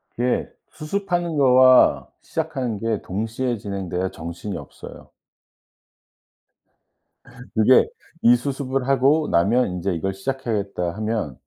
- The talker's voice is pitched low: Yes, low, 115 Hz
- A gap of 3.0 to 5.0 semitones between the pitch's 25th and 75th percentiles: No, wide, 5.4 semitones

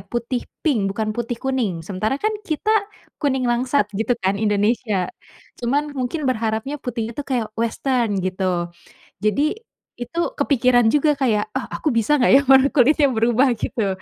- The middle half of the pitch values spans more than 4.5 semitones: No, average, 3.9 semitones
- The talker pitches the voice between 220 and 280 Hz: Yes, high, 240 Hz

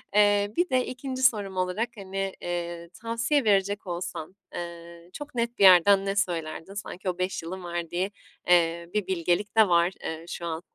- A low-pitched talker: No, medium, 185 Hz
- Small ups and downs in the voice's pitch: No, average, 3.2 semitones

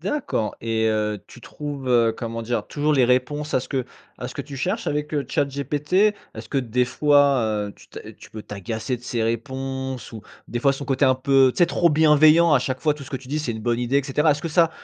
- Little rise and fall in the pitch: No, average, 3.5 semitones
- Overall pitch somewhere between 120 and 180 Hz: Yes, low, 135 Hz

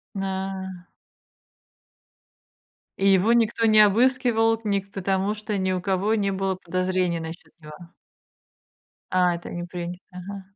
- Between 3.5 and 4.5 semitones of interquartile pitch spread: No, narrow, 2.5 semitones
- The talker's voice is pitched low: No, high, 190 Hz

